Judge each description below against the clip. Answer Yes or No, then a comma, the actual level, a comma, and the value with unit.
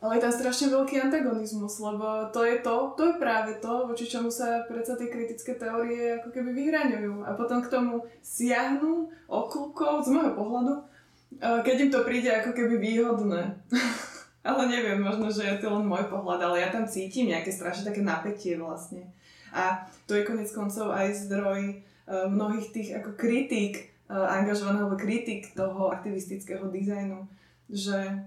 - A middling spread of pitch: Yes, average, 3.5 semitones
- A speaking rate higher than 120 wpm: Yes, average, 160 wpm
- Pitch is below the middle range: No, high, 220 Hz